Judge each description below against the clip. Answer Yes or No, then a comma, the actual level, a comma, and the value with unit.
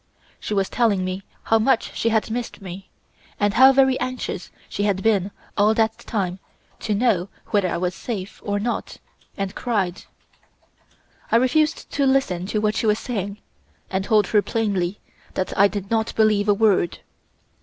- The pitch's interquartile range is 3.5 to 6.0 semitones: No, average, 2.8 semitones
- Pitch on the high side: Yes, high, 210 Hz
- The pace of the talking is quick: No, average, 170 wpm